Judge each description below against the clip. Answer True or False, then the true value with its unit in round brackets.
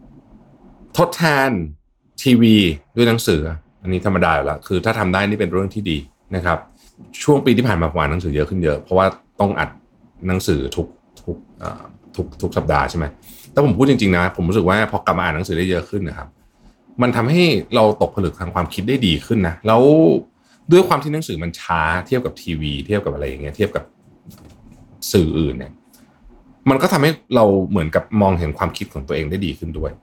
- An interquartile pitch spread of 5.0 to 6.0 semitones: True (5.3 semitones)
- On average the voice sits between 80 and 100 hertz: True (95 Hz)